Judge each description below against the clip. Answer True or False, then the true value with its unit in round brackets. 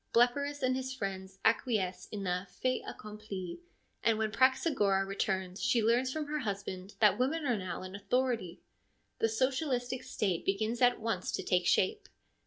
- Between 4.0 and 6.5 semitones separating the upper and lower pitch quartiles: True (4.8 semitones)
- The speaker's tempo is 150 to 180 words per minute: True (160 wpm)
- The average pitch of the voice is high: True (220 Hz)